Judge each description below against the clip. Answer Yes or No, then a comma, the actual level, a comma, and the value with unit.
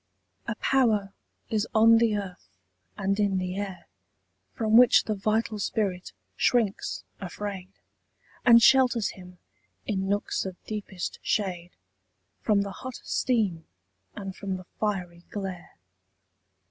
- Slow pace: Yes, slow, 120 wpm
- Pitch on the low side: No, high, 200 Hz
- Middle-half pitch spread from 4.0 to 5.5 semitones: No, average, 2.8 semitones